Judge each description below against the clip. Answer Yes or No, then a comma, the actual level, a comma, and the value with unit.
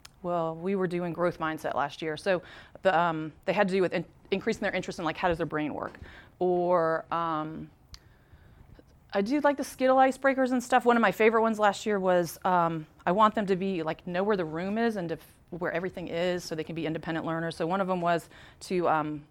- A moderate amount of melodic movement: Yes, average, 3.3 semitones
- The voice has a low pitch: No, medium, 180 Hz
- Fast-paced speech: Yes, fast, 235 wpm